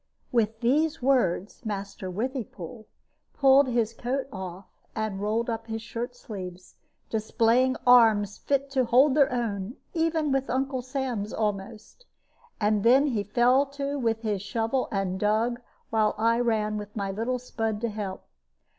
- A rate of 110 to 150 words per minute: Yes, average, 145 wpm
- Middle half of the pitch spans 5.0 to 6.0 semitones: No, average, 3.6 semitones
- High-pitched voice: Yes, high, 230 Hz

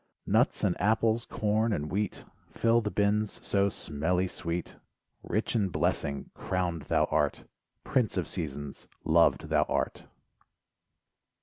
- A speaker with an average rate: No, slow, 125 wpm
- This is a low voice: Yes, low, 100 Hz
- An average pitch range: Yes, average, 4.4 semitones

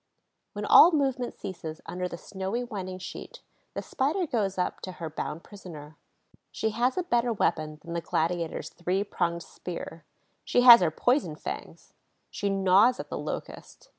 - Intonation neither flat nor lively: No, wide, 5.9 semitones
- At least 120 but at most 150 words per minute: No, average, 165 wpm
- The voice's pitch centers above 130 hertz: Yes, high, 190 Hz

